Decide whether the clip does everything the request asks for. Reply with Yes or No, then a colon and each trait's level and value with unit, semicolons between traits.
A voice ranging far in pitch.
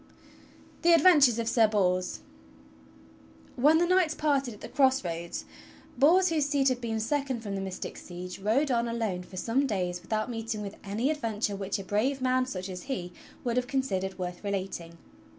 Yes: wide, 5.9 semitones